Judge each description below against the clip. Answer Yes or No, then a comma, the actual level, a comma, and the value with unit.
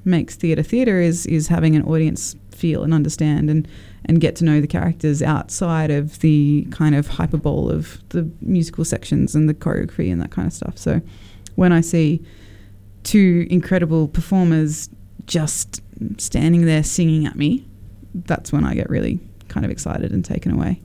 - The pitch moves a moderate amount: No, wide, 7.4 semitones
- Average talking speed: Yes, average, 175 wpm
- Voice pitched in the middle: Yes, medium, 155 Hz